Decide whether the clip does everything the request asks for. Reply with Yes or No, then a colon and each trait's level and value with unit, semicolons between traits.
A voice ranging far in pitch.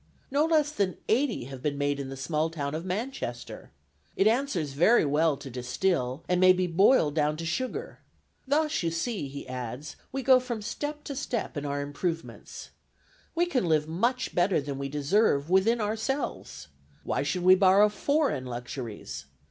Yes: wide, 8.6 semitones